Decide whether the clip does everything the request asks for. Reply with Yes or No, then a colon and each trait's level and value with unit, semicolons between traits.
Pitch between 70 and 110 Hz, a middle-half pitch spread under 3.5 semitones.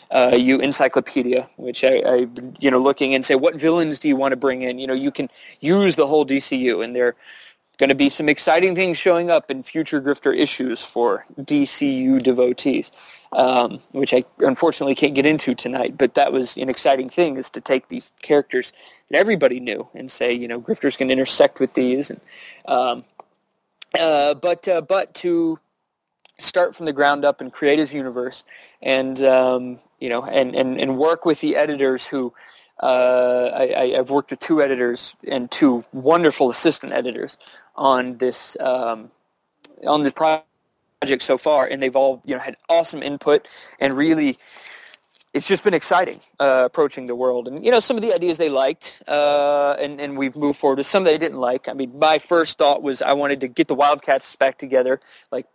No: medium, 140 Hz; average, 3.1 semitones